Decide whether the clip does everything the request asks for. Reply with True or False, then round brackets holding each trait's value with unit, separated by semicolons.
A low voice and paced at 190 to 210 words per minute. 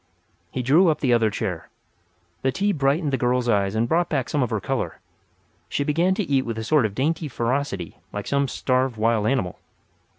True (130 Hz; 200 wpm)